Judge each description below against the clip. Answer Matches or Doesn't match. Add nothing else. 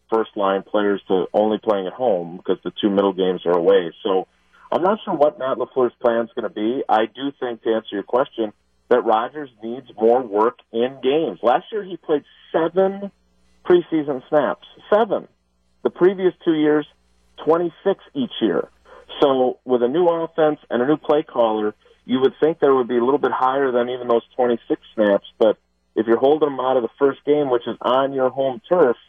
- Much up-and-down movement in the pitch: Matches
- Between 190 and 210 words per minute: Matches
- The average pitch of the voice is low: Matches